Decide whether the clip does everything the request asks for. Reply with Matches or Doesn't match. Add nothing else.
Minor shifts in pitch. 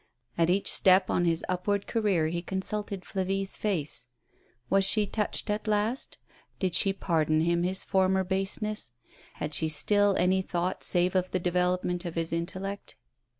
Matches